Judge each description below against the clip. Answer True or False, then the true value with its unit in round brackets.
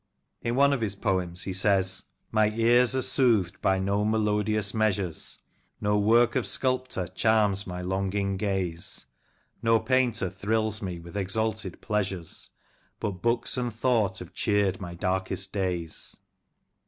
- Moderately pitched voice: False (100 Hz)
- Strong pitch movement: False (2.9 semitones)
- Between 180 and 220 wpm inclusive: False (140 wpm)